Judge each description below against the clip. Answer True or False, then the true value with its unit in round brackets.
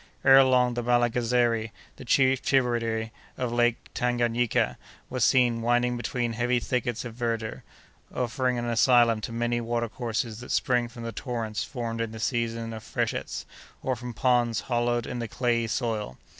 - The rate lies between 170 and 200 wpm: False (160 wpm)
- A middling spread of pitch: False (1.1 semitones)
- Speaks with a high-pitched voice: False (120 Hz)